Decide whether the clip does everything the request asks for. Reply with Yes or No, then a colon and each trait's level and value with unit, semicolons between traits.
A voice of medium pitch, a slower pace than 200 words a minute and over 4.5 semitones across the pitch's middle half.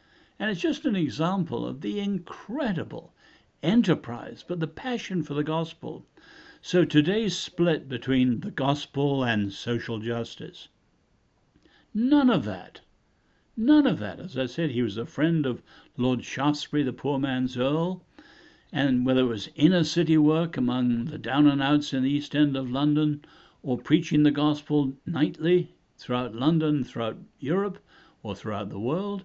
Yes: medium, 150 Hz; average, 155 wpm; average, 5.1 semitones